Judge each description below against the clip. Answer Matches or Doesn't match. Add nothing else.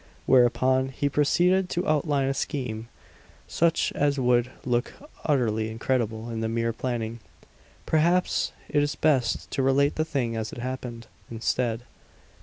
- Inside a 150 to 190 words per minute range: Doesn't match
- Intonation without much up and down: Doesn't match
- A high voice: Doesn't match